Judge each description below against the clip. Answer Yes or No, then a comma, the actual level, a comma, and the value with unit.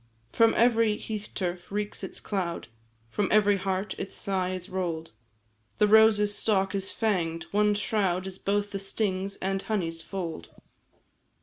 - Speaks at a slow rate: No, average, 145 wpm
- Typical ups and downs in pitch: No, narrow, 2.1 semitones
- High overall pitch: Yes, high, 195 Hz